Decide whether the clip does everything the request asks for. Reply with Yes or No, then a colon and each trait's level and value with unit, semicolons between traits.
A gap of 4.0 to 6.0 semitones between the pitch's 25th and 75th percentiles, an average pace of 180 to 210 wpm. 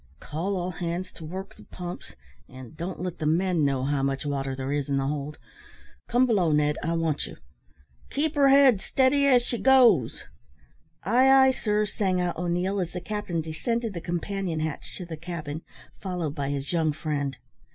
Yes: average, 5.3 semitones; average, 185 wpm